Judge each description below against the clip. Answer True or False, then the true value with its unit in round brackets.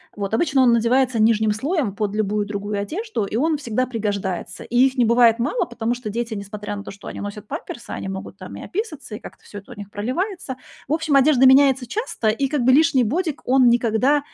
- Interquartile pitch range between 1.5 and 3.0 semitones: False (4.6 semitones)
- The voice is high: True (240 Hz)